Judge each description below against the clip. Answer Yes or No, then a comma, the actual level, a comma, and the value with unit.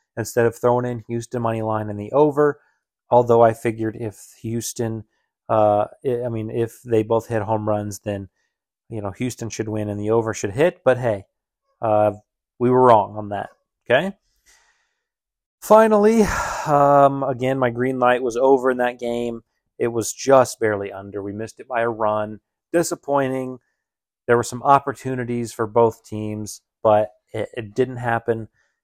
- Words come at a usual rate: Yes, average, 165 wpm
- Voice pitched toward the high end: No, low, 115 Hz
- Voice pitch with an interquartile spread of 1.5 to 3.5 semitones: Yes, average, 3.1 semitones